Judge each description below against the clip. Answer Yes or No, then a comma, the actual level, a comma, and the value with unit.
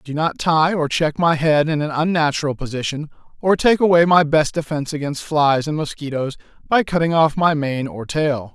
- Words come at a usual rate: Yes, average, 195 wpm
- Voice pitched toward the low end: No, medium, 155 Hz